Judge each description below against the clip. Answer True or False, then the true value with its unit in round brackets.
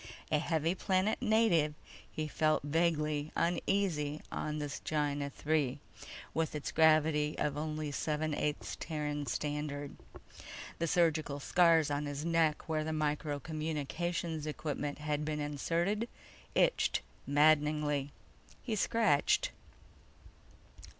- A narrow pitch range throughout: True (1.7 semitones)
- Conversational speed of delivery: False (110 wpm)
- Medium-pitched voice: True (155 Hz)